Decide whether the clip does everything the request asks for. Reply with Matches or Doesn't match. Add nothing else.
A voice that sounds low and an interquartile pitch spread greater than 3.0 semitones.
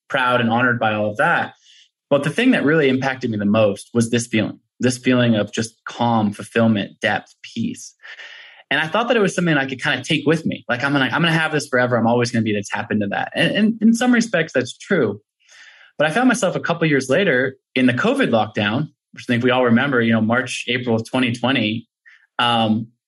Matches